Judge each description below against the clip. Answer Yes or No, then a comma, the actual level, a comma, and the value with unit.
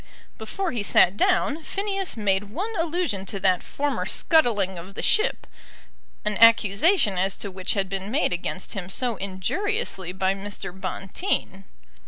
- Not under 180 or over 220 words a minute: No, average, 150 wpm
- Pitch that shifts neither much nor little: No, wide, 9.0 semitones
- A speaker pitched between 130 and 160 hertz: No, high, 205 Hz